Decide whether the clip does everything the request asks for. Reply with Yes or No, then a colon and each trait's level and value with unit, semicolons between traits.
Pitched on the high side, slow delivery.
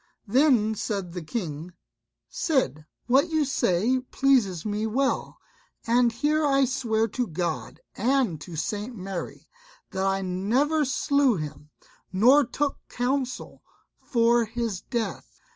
Yes: high, 230 Hz; slow, 125 wpm